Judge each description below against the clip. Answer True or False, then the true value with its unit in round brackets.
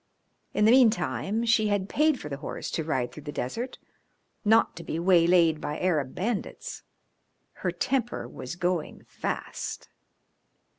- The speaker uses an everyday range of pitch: False (6.4 semitones)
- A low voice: False (185 Hz)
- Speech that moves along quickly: False (145 wpm)